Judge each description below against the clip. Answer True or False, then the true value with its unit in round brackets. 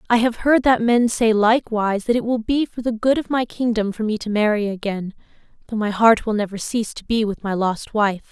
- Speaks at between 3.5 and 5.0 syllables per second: False (5.6 syllables/s)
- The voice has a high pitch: True (220 Hz)